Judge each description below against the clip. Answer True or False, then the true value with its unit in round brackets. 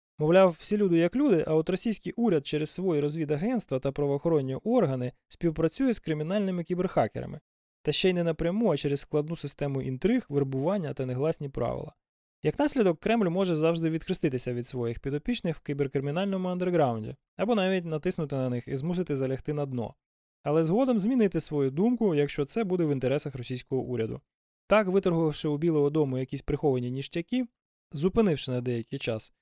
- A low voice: False (155 Hz)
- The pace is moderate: False (160 wpm)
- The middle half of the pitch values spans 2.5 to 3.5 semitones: False (5.0 semitones)